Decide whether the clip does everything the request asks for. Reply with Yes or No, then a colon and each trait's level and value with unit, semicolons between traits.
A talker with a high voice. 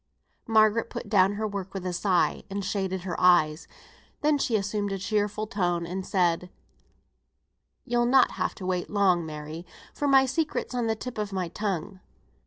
Yes: high, 200 Hz